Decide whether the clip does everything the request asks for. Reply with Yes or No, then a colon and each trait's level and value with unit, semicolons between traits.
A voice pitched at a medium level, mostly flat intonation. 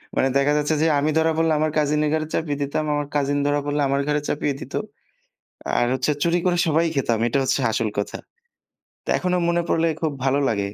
Yes: medium, 145 Hz; narrow, 2.3 semitones